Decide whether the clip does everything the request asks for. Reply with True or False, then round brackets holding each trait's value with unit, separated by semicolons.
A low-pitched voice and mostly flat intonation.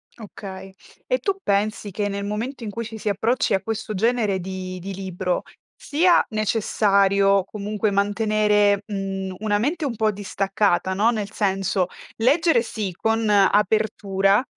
False (205 Hz; 2.2 semitones)